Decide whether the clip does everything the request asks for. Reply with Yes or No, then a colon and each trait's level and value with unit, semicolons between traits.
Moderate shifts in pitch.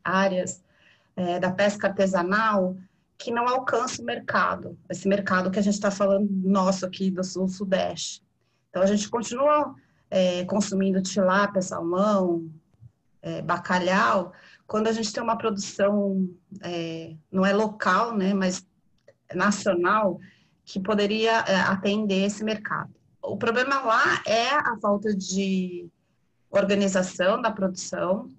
No: narrow, 2.1 semitones